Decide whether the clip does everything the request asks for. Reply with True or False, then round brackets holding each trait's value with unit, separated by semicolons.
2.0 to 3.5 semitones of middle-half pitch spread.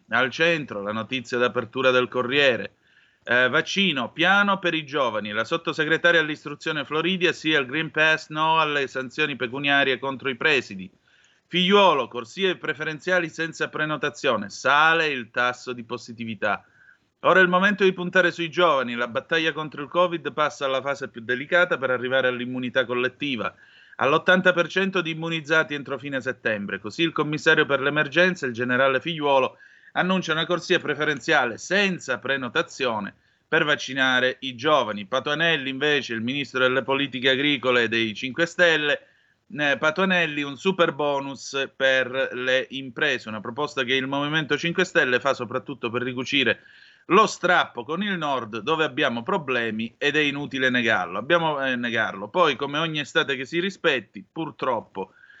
False (4.1 semitones)